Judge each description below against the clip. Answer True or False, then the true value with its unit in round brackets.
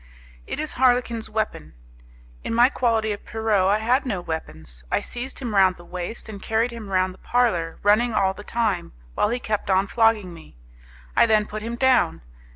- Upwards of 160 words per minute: True (190 wpm)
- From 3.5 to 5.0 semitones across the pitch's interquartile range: True (3.9 semitones)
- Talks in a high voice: True (215 Hz)